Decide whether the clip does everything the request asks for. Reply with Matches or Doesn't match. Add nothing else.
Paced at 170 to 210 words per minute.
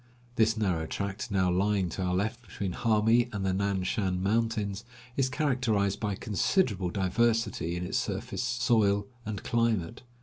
Doesn't match